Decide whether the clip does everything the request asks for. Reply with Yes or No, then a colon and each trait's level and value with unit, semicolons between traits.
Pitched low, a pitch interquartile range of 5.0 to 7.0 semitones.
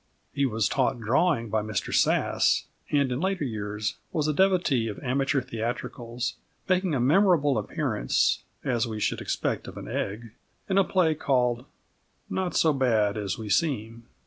Yes: low, 125 Hz; average, 5.3 semitones